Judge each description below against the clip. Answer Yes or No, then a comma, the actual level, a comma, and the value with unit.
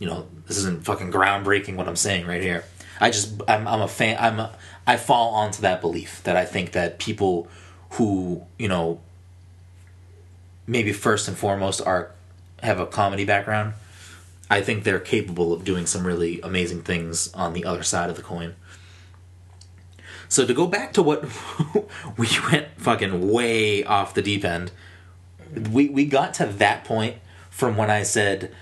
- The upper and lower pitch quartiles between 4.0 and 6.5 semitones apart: No, average, 3.0 semitones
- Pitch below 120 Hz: Yes, very low, 95 Hz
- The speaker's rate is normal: Yes, average, 170 wpm